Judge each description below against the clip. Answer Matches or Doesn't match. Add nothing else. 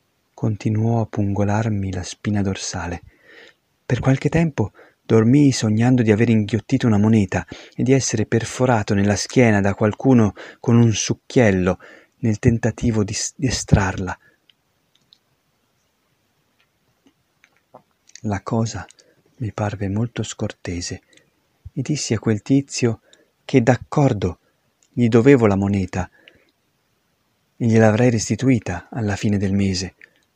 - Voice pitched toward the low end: Matches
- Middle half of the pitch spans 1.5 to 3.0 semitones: Doesn't match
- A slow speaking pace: Matches